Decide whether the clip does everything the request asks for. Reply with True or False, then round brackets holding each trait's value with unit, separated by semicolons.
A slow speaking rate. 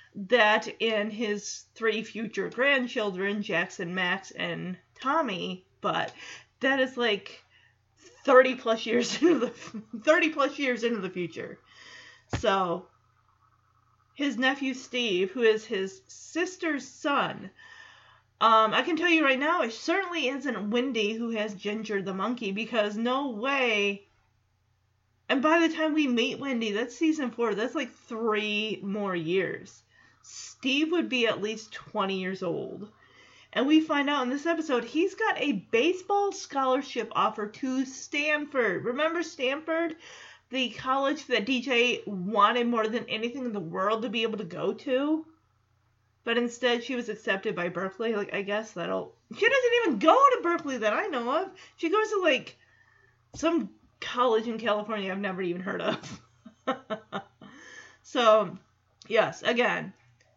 False (145 wpm)